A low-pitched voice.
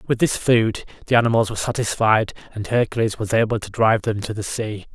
Yes: low, 110 Hz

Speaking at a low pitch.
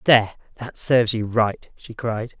Yes: low, 115 Hz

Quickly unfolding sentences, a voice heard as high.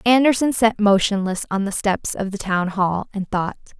No: average, 190 wpm; high, 205 Hz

